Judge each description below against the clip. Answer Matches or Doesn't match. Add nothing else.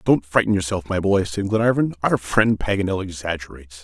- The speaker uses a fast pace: Doesn't match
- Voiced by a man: Matches